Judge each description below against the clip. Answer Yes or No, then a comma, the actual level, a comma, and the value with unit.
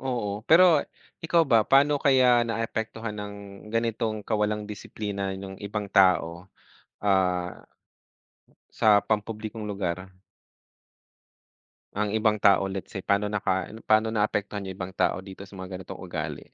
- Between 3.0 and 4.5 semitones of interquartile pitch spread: No, narrow, 2.5 semitones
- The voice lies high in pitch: No, low, 105 Hz